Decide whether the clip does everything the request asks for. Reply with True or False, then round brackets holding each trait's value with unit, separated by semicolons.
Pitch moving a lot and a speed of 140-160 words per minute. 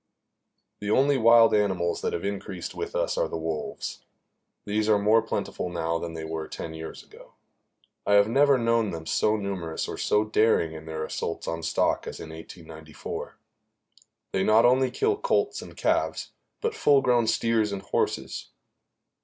False (5.9 semitones; 170 wpm)